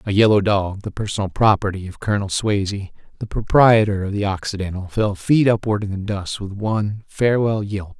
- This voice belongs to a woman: No, male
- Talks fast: No, average, 180 wpm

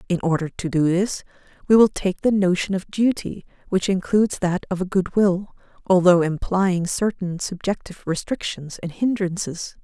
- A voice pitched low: No, medium, 185 Hz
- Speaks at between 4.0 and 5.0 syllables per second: Yes, 4.8 syllables/s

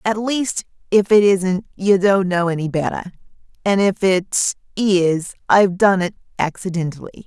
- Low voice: No, high, 190 Hz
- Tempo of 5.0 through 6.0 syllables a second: No, 4.4 syllables/s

